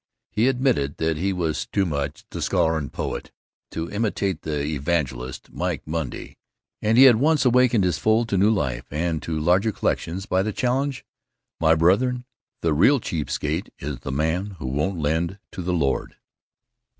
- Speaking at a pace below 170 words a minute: No, average, 175 wpm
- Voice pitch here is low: Yes, very low, 85 Hz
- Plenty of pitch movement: Yes, wide, 6.1 semitones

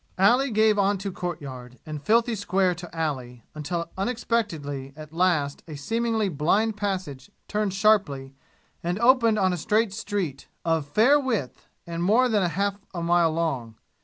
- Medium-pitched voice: Yes, medium, 180 Hz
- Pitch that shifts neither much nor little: No, wide, 5.8 semitones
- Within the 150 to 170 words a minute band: Yes, average, 155 wpm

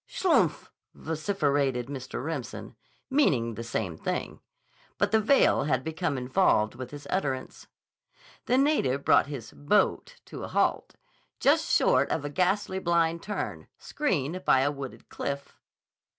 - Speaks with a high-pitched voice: No, medium, 145 Hz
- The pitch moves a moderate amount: No, wide, 6.4 semitones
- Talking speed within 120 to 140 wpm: Yes, slow, 135 wpm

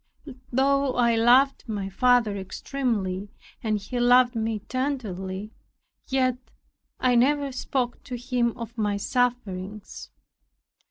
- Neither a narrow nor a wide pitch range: Yes, average, 3.4 semitones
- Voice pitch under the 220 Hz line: No, high, 240 Hz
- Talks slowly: Yes, slow, 110 wpm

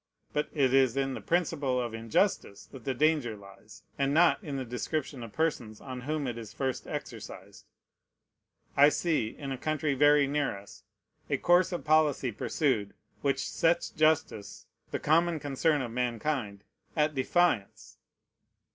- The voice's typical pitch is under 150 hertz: Yes, medium, 140 Hz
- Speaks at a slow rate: No, average, 155 wpm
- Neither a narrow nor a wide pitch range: Yes, average, 4.6 semitones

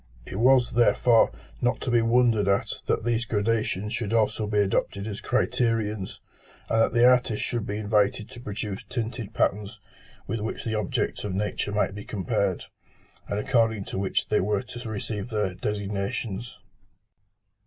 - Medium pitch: No, low, 110 Hz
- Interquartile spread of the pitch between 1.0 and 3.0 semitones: Yes, narrow, 2.4 semitones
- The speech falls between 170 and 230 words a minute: No, average, 160 wpm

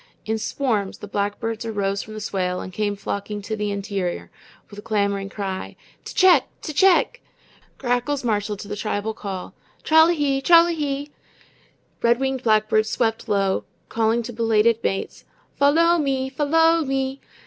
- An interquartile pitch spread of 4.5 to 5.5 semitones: Yes, average, 5.1 semitones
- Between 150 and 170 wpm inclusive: Yes, average, 160 wpm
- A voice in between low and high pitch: No, high, 225 Hz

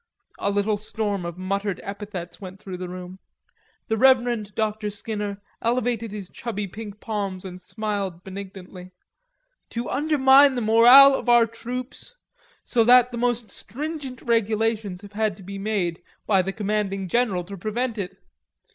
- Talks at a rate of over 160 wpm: No, average, 150 wpm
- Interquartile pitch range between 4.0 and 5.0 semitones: No, average, 3.4 semitones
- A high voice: Yes, high, 210 Hz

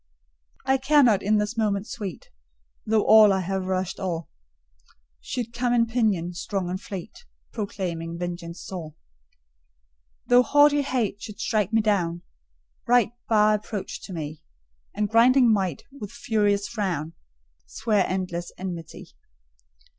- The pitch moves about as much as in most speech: Yes, average, 4.0 semitones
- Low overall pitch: No, high, 205 Hz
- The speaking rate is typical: No, slow, 130 wpm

